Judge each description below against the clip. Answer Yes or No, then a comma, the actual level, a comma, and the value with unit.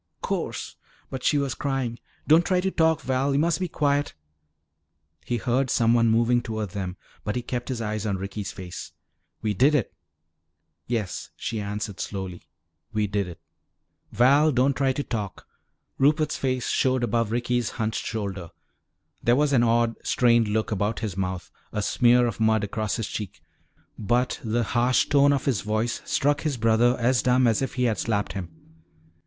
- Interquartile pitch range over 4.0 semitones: No, average, 3.7 semitones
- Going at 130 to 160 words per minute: No, average, 170 wpm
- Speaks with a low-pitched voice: Yes, low, 120 Hz